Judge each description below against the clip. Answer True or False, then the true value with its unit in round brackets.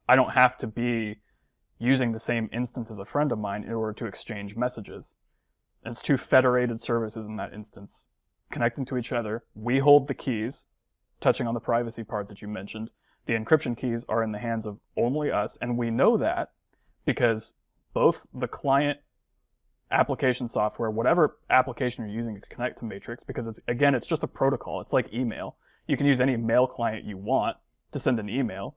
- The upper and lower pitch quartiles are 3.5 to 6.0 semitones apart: False (2.4 semitones)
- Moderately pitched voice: False (115 Hz)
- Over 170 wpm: True (195 wpm)